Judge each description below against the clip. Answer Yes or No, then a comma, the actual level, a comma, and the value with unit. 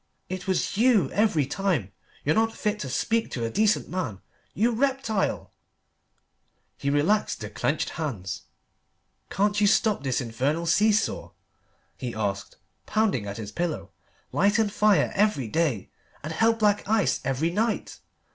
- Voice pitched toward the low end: No, medium, 185 Hz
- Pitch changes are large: Yes, wide, 8.0 semitones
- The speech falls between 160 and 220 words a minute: No, average, 145 wpm